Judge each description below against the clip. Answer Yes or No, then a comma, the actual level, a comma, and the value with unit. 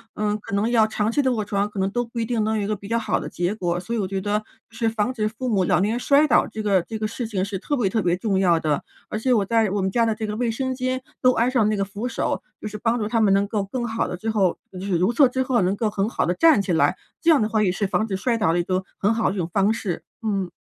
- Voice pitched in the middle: No, high, 215 Hz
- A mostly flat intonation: No, average, 3.0 semitones